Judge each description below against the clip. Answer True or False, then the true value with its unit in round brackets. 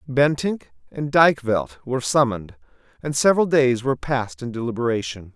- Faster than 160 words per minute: False (135 wpm)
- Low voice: True (125 Hz)